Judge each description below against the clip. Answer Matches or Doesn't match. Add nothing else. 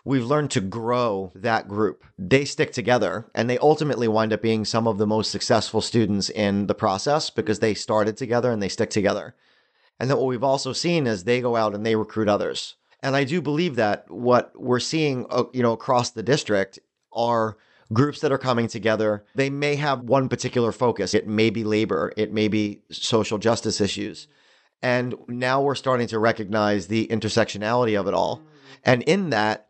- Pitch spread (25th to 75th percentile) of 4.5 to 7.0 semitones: Doesn't match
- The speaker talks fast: Doesn't match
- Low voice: Matches